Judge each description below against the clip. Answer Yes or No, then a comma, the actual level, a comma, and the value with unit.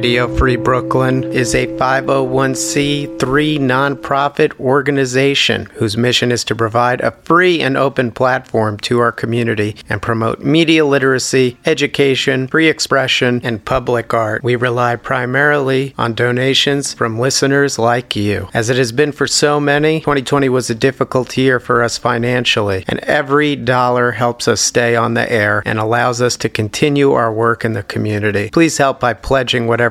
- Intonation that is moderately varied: Yes, average, 3.0 semitones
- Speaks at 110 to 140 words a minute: No, average, 160 wpm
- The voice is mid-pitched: No, low, 125 Hz